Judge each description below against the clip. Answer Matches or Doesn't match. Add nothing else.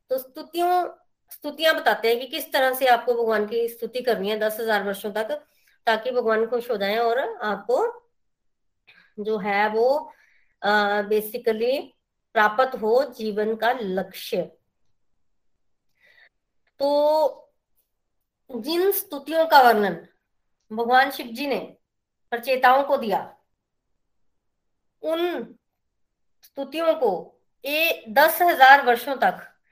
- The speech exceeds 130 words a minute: Doesn't match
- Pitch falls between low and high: Doesn't match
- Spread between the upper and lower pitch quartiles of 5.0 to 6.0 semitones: Matches